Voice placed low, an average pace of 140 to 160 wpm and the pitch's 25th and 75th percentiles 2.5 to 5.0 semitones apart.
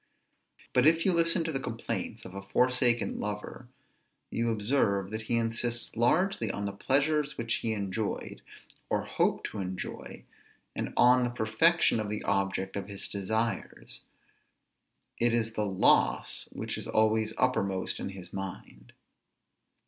Yes: low, 110 Hz; average, 145 wpm; average, 3.8 semitones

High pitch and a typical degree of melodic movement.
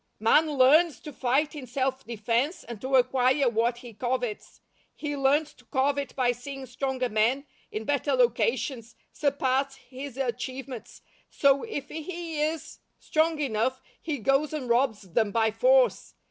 Yes: very high, 265 Hz; average, 3.1 semitones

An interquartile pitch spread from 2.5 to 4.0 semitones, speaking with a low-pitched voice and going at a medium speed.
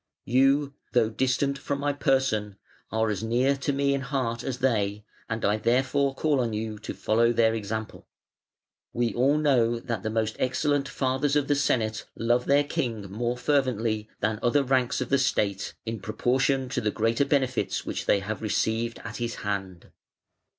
Yes: average, 3.6 semitones; low, 120 Hz; average, 175 wpm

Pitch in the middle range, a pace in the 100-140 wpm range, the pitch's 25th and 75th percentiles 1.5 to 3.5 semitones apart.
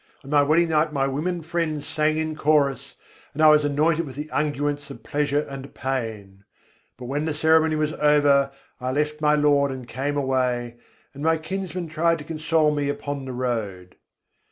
No: medium, 145 Hz; average, 180 wpm; narrow, 2.4 semitones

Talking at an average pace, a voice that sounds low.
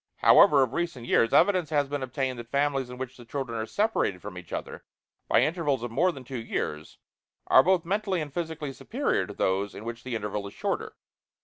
No: fast, 210 wpm; low, 130 Hz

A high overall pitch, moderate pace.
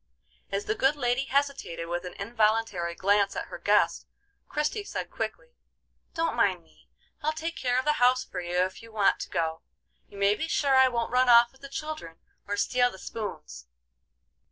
Yes: high, 235 Hz; average, 190 wpm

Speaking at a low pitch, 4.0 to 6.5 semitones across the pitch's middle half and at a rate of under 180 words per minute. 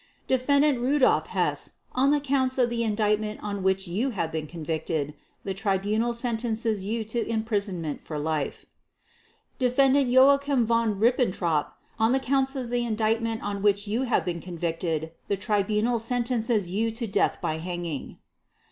No: high, 220 Hz; average, 4.4 semitones; average, 150 wpm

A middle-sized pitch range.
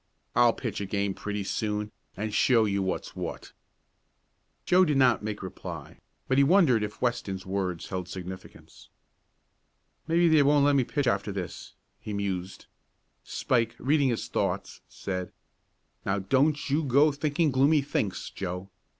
No: wide, 6.2 semitones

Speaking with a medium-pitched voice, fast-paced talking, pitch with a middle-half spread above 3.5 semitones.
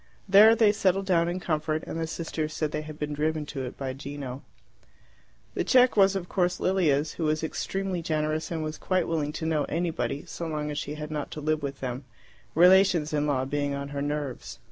No: medium, 155 Hz; fast, 210 wpm; average, 3.2 semitones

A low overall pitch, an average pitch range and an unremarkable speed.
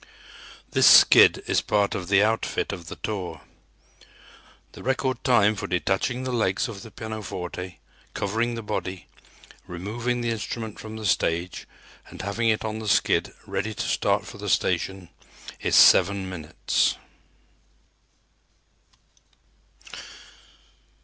No: low, 105 Hz; average, 3.2 semitones; slow, 125 wpm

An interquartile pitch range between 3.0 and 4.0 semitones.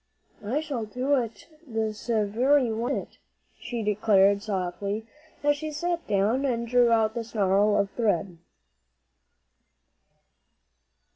Yes: average, 3.4 semitones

